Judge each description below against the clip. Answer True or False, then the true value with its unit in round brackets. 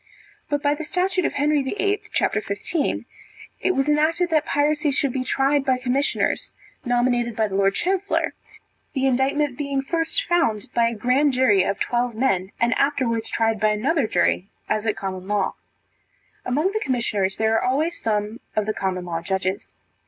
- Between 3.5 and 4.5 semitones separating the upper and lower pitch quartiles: False (5.5 semitones)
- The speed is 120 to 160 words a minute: False (175 wpm)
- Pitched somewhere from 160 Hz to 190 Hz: False (255 Hz)